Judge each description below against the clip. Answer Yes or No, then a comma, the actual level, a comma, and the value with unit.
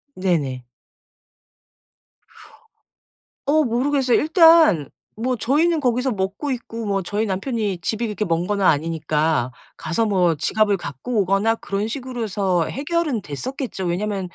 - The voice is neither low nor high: No, high, 210 Hz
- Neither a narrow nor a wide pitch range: No, wide, 6.0 semitones